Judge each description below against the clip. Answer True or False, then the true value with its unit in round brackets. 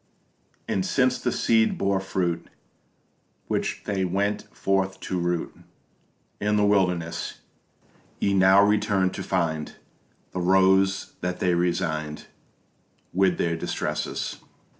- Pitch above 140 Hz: False (95 Hz)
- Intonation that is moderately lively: False (2.1 semitones)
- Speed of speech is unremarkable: False (115 wpm)